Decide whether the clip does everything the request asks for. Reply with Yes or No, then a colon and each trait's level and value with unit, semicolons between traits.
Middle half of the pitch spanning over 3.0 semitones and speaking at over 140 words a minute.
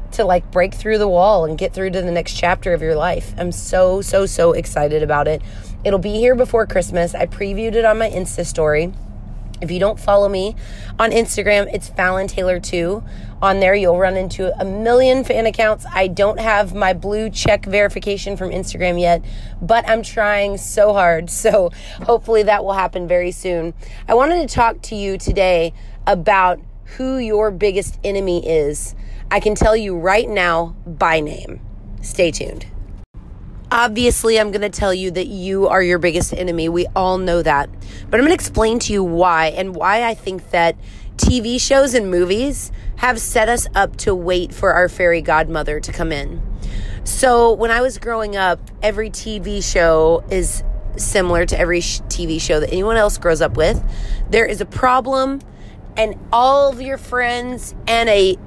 Yes: average, 4.4 semitones; average, 185 wpm